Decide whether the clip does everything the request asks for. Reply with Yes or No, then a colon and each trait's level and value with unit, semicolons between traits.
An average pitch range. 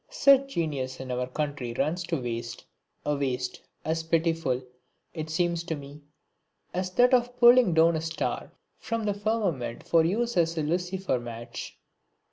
No: wide, 6.0 semitones